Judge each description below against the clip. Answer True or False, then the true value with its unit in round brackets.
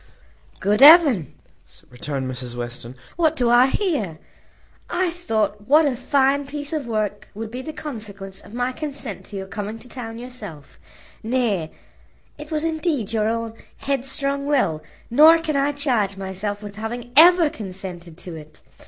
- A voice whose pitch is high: True (230 Hz)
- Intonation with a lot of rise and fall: True (6.5 semitones)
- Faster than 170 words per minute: False (155 wpm)